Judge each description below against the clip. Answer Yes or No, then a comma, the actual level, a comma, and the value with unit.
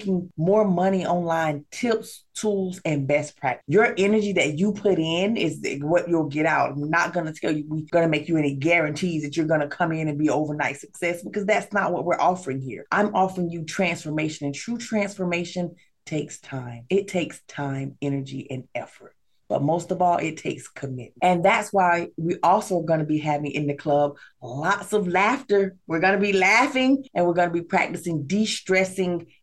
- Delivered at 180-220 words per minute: Yes, average, 200 wpm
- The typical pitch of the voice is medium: Yes, medium, 170 Hz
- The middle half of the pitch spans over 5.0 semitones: No, average, 4.1 semitones